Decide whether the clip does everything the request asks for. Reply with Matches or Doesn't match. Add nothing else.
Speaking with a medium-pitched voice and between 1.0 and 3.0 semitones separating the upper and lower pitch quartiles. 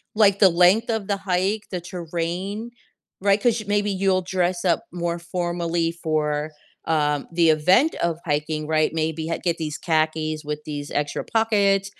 Doesn't match